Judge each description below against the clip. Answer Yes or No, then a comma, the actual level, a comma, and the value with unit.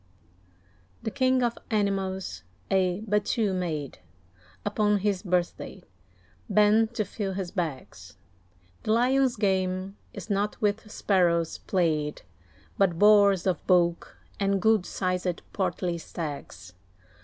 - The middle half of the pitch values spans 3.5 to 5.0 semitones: No, average, 3.0 semitones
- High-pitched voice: Yes, high, 195 Hz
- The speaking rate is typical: No, slow, 110 wpm